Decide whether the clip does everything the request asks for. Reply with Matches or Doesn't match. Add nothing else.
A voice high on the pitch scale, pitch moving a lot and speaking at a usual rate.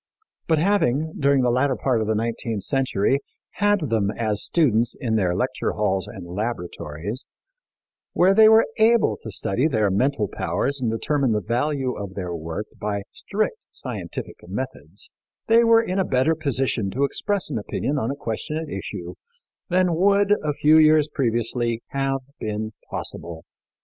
Doesn't match